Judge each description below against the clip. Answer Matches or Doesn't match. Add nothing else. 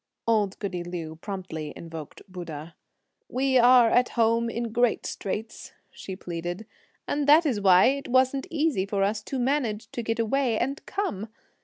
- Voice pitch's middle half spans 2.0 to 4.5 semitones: Doesn't match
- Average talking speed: Matches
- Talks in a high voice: Matches